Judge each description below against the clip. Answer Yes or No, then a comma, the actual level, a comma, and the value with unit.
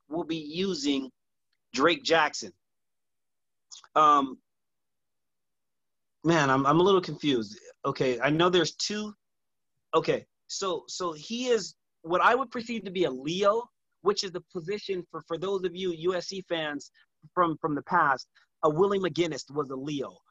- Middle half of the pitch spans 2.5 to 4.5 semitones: Yes, average, 3.9 semitones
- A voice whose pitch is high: No, medium, 180 Hz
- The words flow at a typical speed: Yes, average, 150 wpm